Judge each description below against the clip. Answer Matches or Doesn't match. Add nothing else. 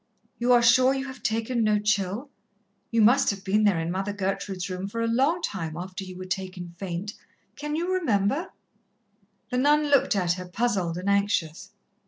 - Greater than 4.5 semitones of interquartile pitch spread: Matches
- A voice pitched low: Doesn't match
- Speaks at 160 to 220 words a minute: Matches